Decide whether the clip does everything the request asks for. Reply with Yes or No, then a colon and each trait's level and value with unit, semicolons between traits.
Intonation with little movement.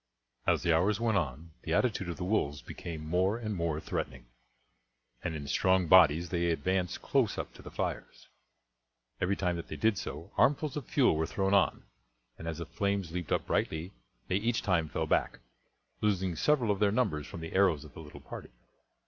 No: average, 3.7 semitones